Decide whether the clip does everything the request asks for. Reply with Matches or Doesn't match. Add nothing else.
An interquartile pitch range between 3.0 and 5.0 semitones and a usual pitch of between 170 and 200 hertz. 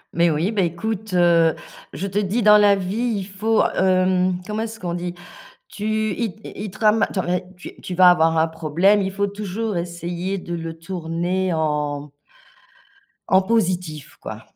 Matches